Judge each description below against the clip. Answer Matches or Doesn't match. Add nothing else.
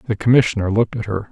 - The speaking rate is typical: Doesn't match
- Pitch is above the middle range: Doesn't match